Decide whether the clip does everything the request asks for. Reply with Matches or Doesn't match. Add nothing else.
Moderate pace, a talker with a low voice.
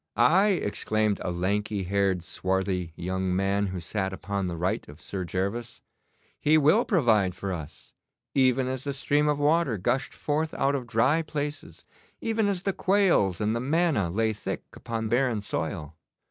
Matches